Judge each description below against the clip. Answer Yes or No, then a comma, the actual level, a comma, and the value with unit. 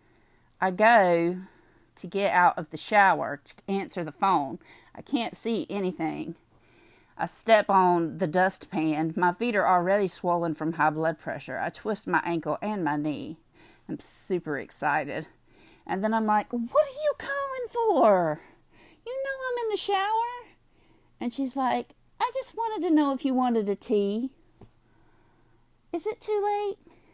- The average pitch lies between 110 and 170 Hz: No, high, 210 Hz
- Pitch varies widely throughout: Yes, wide, 8.6 semitones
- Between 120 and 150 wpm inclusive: No, average, 160 wpm